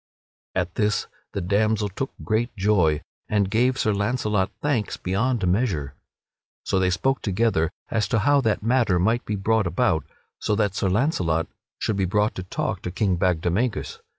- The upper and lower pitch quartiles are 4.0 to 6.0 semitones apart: No, average, 3.5 semitones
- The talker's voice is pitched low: Yes, low, 105 Hz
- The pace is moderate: Yes, average, 165 wpm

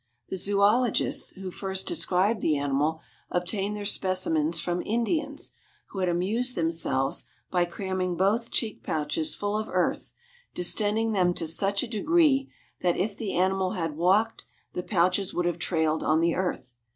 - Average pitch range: Yes, average, 3.6 semitones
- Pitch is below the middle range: No, medium, 185 Hz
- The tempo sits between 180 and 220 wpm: No, average, 155 wpm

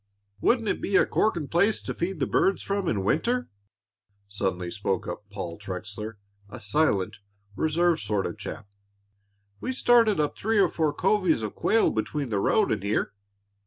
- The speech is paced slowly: No, average, 165 wpm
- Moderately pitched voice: Yes, medium, 150 Hz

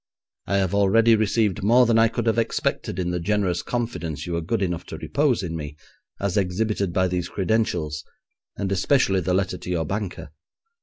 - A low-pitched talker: Yes, very low, 95 Hz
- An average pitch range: Yes, average, 3.9 semitones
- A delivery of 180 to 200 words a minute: Yes, average, 190 wpm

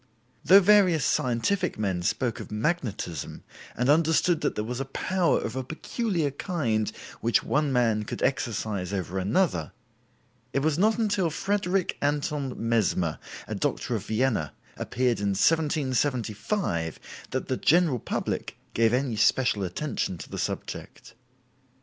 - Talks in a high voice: No, low, 130 Hz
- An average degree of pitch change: No, wide, 7.1 semitones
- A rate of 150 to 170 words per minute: No, slow, 135 wpm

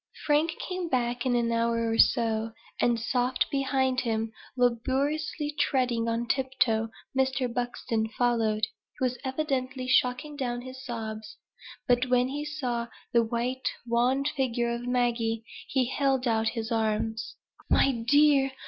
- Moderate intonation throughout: No, narrow, 2.3 semitones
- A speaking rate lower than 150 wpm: Yes, average, 140 wpm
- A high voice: Yes, high, 245 Hz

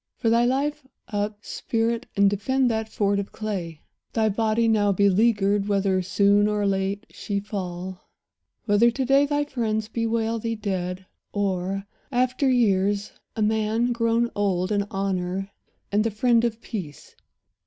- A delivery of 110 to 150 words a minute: Yes, average, 145 wpm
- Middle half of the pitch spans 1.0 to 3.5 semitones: Yes, average, 2.7 semitones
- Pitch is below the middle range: No, high, 210 Hz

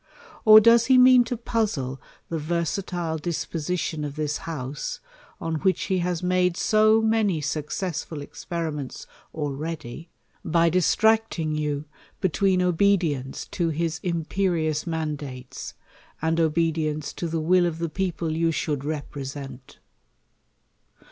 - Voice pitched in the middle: Yes, medium, 165 Hz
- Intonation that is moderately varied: Yes, average, 3.3 semitones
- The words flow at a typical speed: No, slow, 130 wpm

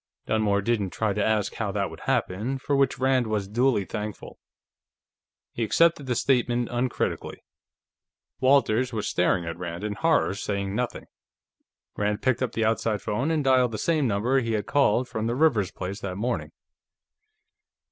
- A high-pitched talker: No, low, 115 Hz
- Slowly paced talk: No, average, 165 wpm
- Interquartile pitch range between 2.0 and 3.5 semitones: No, average, 4.0 semitones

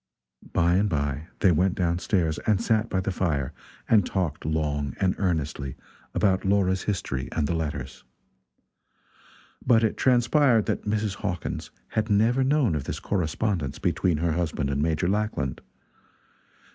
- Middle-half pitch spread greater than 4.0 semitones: Yes, average, 5.3 semitones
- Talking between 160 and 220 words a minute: No, average, 145 wpm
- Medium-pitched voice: No, very low, 90 Hz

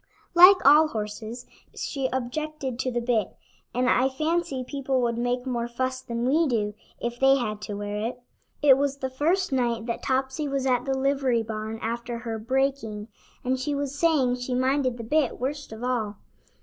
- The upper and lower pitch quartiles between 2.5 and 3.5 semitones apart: Yes, average, 2.8 semitones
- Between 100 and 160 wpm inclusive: No, average, 185 wpm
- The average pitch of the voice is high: Yes, very high, 255 Hz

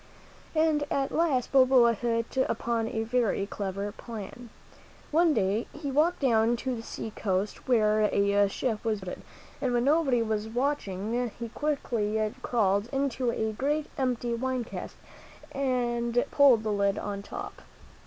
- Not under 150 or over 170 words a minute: Yes, average, 155 wpm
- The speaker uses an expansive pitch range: No, average, 3.7 semitones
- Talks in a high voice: Yes, high, 235 Hz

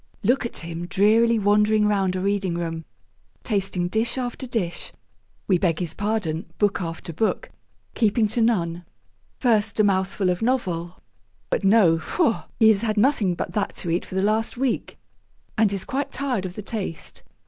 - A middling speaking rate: Yes, average, 170 wpm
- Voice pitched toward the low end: No, high, 205 Hz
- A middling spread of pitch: Yes, average, 4.0 semitones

